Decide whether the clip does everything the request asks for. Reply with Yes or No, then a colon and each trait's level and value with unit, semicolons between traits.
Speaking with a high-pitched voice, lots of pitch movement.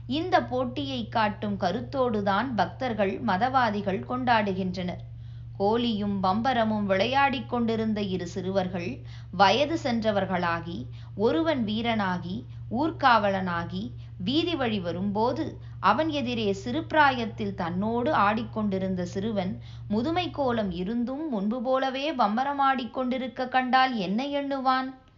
Yes: high, 215 Hz; wide, 5.7 semitones